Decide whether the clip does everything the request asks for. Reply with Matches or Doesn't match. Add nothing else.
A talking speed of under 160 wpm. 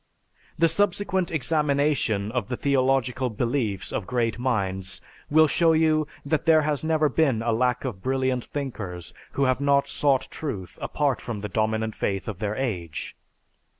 Matches